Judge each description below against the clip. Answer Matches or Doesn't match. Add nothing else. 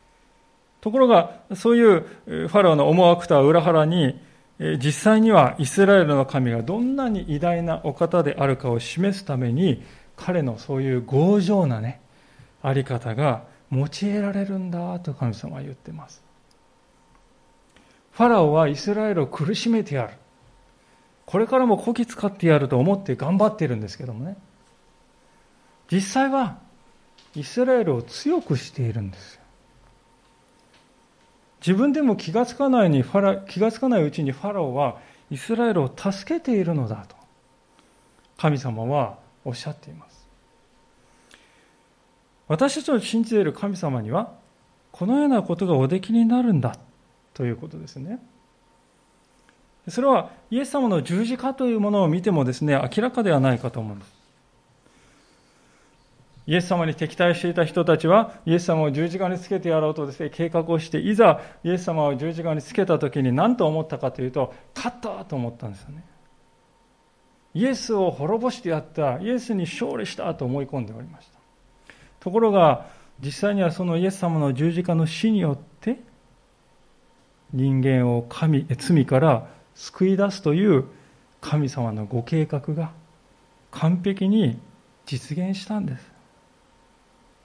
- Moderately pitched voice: Matches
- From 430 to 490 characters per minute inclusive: Doesn't match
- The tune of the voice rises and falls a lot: Matches